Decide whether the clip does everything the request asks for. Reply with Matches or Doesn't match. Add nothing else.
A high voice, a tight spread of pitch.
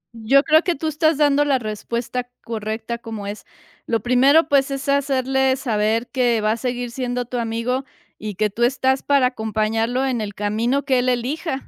Doesn't match